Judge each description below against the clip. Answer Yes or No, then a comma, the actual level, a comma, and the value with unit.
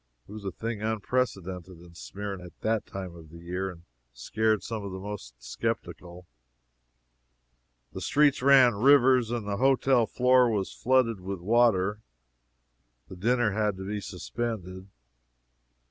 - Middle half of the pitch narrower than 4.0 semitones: No, average, 4.4 semitones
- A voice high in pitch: No, low, 105 Hz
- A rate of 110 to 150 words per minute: Yes, average, 145 wpm